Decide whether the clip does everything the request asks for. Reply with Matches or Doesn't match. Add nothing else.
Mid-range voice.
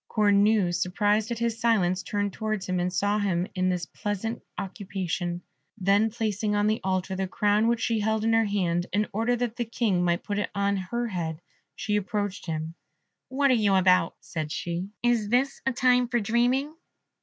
Doesn't match